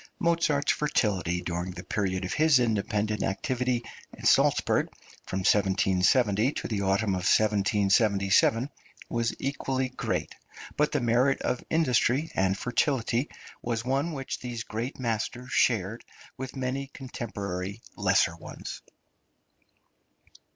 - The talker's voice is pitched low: Yes, low, 115 Hz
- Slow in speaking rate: Yes, slow, 115 wpm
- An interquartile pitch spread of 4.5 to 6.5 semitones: Yes, average, 4.9 semitones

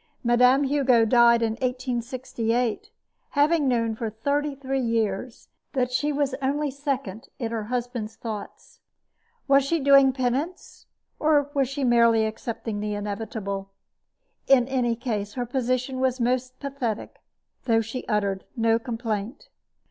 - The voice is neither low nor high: No, high, 245 Hz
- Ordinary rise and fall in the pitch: Yes, average, 3.1 semitones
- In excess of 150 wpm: No, slow, 135 wpm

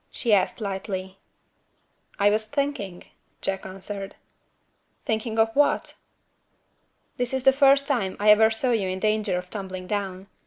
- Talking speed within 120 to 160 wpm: Yes, average, 145 wpm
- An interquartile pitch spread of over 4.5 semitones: No, average, 3.4 semitones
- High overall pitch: Yes, high, 210 Hz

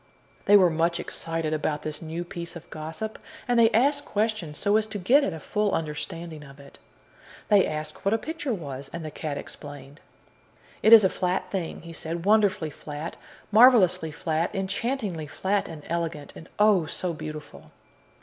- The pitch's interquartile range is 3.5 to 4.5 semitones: No, average, 5.1 semitones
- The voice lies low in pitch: No, medium, 170 Hz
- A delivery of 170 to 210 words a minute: Yes, average, 175 wpm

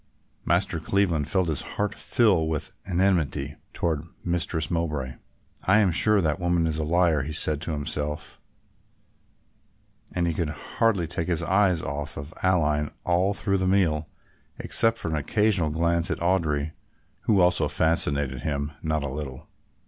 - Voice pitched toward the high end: No, very low, 80 Hz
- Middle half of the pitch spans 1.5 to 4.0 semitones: Yes, average, 3.5 semitones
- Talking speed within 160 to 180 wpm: No, average, 150 wpm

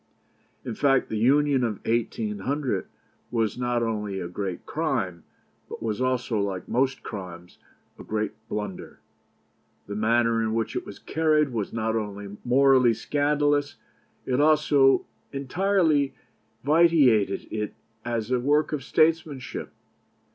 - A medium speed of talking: No, slow, 125 wpm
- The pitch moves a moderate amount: Yes, average, 5.0 semitones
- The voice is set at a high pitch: No, low, 120 Hz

